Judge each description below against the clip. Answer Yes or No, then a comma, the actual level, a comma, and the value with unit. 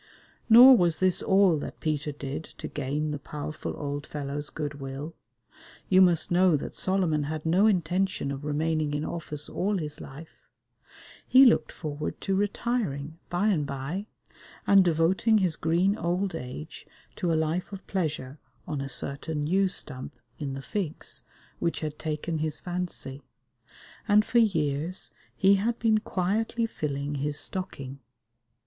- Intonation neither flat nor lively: Yes, average, 4.4 semitones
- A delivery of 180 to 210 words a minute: No, average, 150 wpm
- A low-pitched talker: No, medium, 160 Hz